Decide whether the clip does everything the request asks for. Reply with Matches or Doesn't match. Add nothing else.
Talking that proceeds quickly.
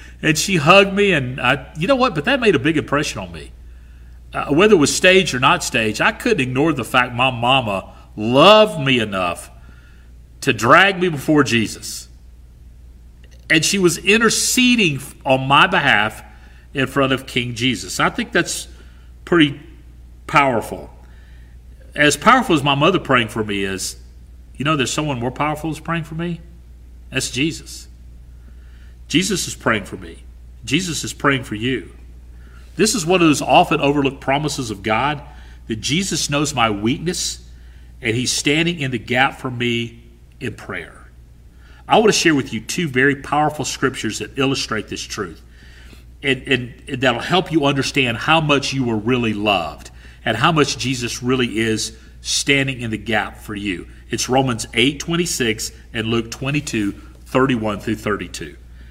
Doesn't match